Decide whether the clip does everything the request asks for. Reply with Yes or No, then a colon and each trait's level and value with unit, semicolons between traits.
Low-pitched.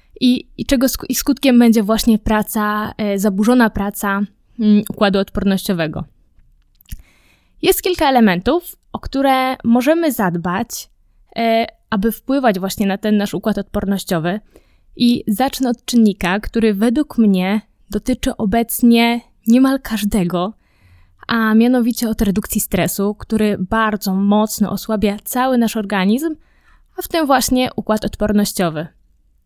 No: high, 220 Hz